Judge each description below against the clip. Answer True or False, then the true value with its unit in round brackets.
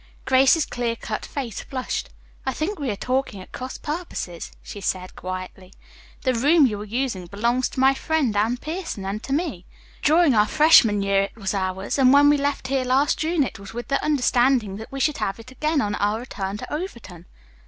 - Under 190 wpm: False (205 wpm)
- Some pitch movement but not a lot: False (5.7 semitones)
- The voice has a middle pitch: False (250 Hz)